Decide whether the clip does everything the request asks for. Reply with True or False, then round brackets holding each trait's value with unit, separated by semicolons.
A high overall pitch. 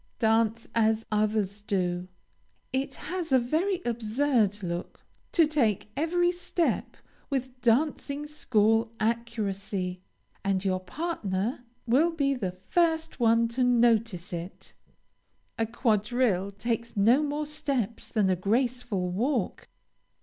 True (230 Hz)